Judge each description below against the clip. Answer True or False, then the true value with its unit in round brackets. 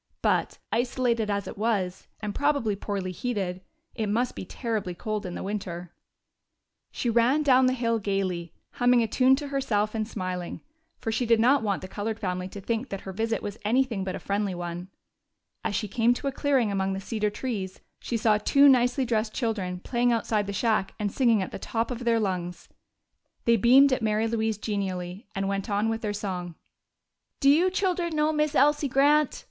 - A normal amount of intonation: True (4.0 semitones)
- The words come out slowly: False (195 wpm)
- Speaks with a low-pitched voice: False (220 Hz)